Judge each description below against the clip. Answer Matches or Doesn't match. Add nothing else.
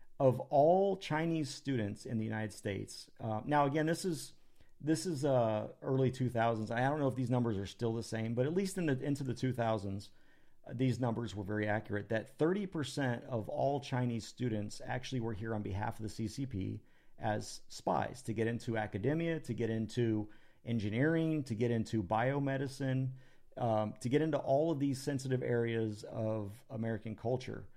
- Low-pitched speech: Matches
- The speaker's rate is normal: Matches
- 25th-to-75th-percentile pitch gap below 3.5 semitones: Doesn't match